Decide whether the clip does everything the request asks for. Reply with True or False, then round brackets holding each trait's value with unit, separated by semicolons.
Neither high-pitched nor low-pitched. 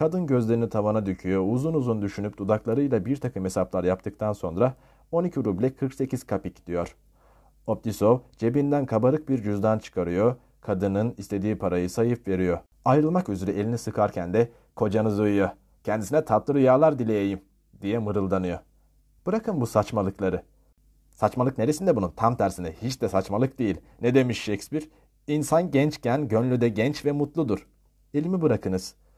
False (110 Hz)